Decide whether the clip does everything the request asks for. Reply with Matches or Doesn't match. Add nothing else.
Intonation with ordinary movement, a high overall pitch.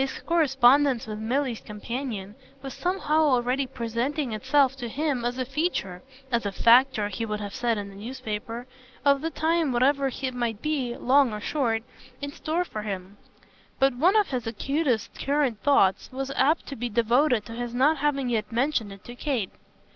Matches